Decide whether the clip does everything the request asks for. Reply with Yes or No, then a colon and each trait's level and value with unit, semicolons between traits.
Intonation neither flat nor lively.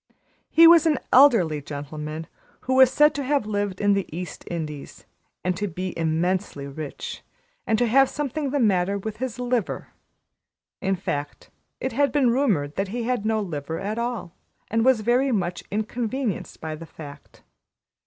No: wide, 7.2 semitones